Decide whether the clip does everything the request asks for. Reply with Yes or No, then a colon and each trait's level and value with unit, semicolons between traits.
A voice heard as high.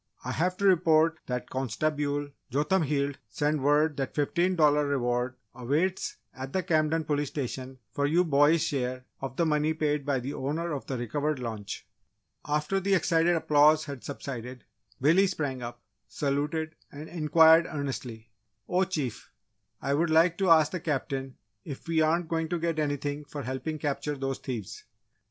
No: medium, 150 Hz